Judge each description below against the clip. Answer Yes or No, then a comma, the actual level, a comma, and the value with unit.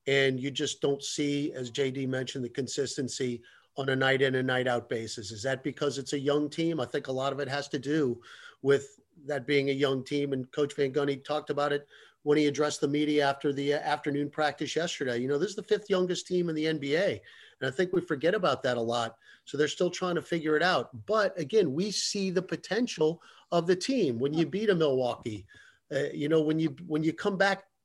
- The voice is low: No, medium, 145 Hz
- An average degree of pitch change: Yes, average, 3.0 semitones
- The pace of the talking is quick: Yes, fast, 235 wpm